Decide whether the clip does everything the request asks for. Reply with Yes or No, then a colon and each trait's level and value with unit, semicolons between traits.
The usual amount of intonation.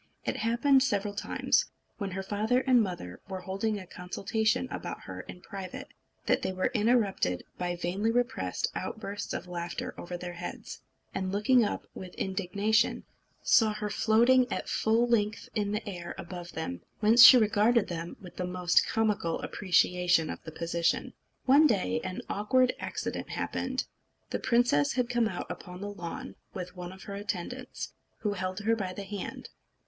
Yes: average, 3.8 semitones